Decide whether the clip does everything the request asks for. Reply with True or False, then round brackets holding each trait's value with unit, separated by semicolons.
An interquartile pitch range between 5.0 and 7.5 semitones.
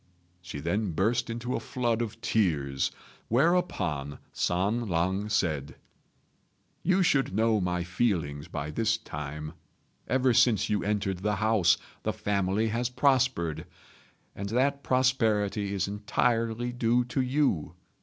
True (5.5 semitones)